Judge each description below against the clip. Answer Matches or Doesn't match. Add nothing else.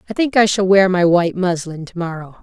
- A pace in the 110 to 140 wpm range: Doesn't match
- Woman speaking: Matches